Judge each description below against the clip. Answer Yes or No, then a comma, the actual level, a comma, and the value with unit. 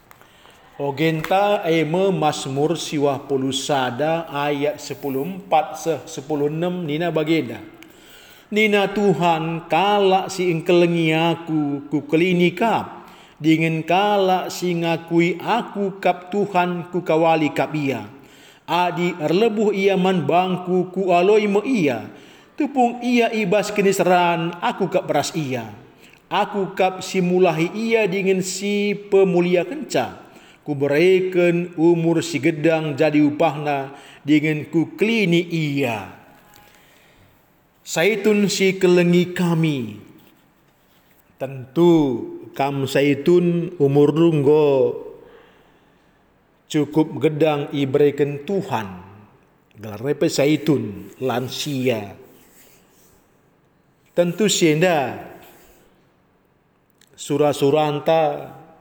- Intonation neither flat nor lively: Yes, average, 4.2 semitones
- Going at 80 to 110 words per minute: Yes, average, 90 wpm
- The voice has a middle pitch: Yes, medium, 165 Hz